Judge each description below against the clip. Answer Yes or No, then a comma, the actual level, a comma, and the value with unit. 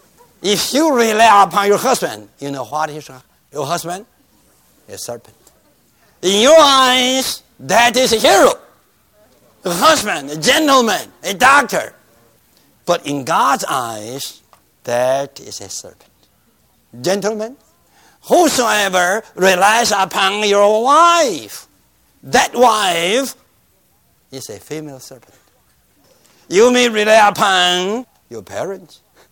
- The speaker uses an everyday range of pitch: No, wide, 8.0 semitones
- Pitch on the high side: Yes, high, 200 Hz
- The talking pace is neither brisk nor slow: No, slow, 110 wpm